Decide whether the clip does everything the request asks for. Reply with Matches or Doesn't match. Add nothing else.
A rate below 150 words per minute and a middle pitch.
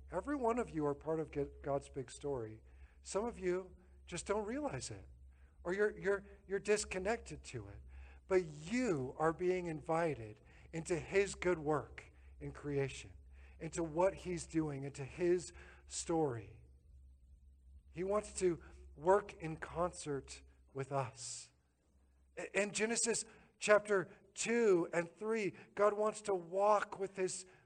Matches